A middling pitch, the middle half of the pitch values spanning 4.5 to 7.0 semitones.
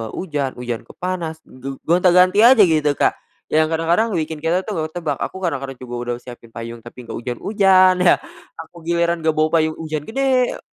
Yes: medium, 160 Hz; average, 5.0 semitones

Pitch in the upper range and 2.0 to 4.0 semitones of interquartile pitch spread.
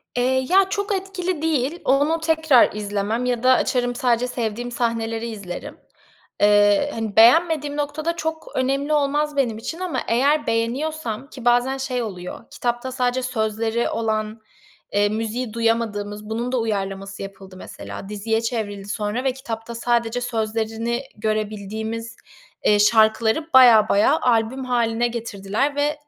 Yes: high, 235 Hz; average, 3.6 semitones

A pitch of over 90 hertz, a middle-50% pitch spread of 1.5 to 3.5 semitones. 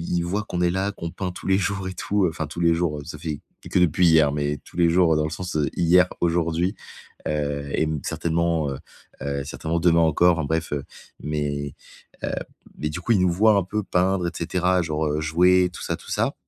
No: very low, 85 Hz; average, 2.9 semitones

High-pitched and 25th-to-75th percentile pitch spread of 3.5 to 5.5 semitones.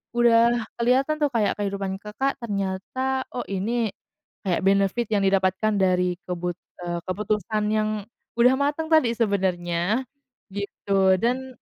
Yes: high, 210 Hz; average, 4.0 semitones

